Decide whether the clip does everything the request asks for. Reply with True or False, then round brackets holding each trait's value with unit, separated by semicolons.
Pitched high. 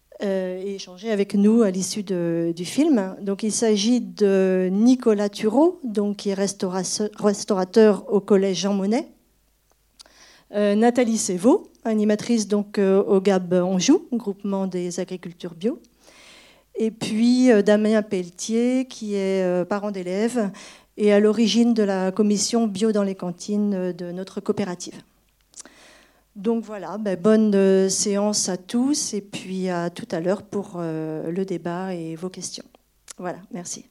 True (205 Hz)